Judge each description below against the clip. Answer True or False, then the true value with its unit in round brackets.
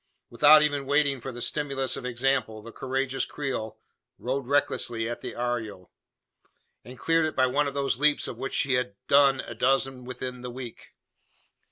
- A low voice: True (130 Hz)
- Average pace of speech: True (175 wpm)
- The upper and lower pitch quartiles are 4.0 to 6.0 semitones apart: False (2.4 semitones)